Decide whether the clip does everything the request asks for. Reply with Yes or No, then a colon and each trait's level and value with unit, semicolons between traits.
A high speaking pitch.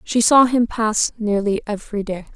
Yes: high, 215 Hz